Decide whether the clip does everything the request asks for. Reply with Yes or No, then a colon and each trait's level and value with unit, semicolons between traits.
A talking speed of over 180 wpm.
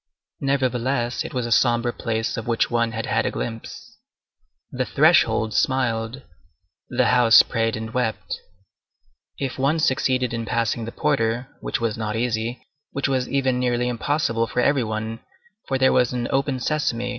No: average, 155 wpm